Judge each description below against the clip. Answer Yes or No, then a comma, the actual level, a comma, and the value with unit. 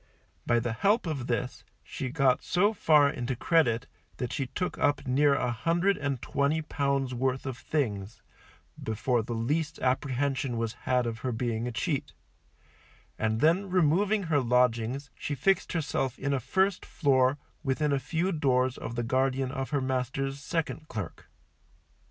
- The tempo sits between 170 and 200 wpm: No, average, 160 wpm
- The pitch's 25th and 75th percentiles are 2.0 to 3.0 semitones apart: No, average, 3.5 semitones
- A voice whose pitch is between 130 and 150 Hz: Yes, low, 135 Hz